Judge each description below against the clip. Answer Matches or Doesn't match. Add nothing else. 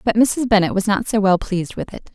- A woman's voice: Matches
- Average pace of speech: Doesn't match